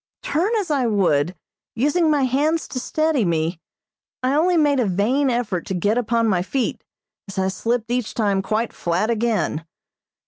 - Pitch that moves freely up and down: Yes, wide, 6.4 semitones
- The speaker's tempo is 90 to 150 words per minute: No, average, 170 wpm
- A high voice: Yes, high, 235 Hz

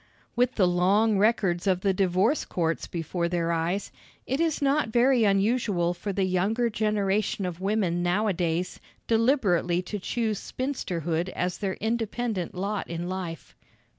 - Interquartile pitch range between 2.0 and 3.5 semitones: No, average, 3.9 semitones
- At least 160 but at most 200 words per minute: No, average, 140 wpm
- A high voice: Yes, high, 195 Hz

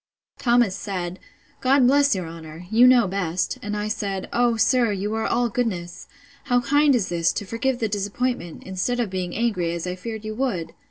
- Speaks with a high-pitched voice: Yes, high, 215 Hz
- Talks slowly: No, average, 185 wpm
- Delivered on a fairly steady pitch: No, average, 4.9 semitones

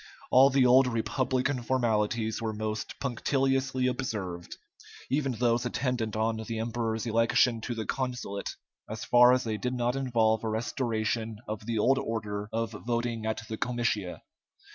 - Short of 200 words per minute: Yes, average, 150 wpm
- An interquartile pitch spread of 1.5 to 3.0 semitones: Yes, narrow, 2.4 semitones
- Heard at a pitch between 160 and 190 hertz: No, low, 115 Hz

